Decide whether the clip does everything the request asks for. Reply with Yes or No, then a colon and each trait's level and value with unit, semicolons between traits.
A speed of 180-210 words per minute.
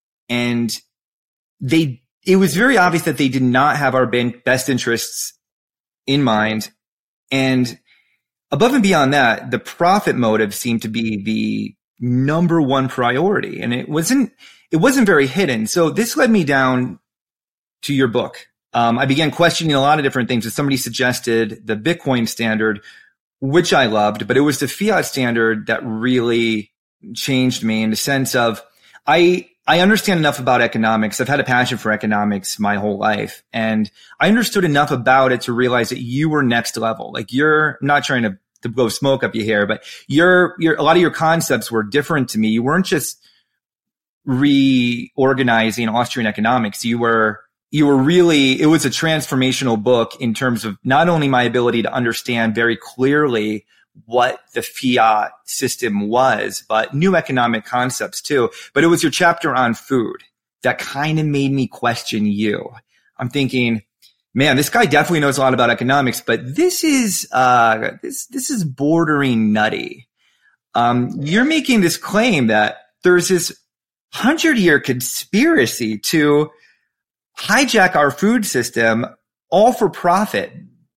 No: average, 165 wpm